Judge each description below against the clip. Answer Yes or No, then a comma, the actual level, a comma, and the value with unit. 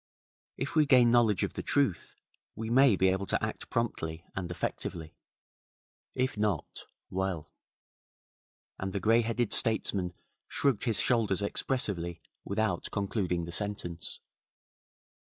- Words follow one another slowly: Yes, slow, 125 wpm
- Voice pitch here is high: No, low, 100 Hz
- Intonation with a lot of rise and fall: No, average, 4.7 semitones